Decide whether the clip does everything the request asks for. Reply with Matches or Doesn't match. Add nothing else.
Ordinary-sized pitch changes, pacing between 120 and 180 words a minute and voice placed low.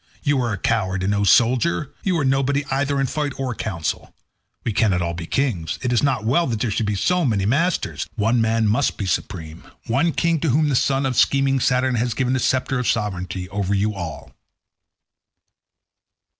Doesn't match